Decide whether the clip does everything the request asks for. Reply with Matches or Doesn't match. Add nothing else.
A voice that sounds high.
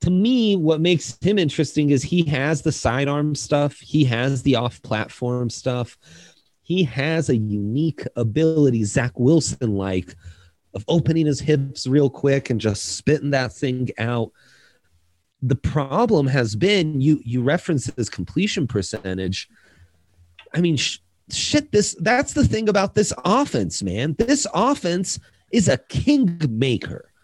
Doesn't match